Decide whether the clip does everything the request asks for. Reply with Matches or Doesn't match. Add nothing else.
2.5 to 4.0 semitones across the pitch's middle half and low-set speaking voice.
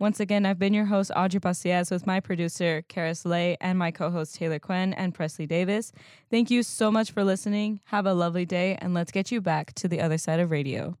Doesn't match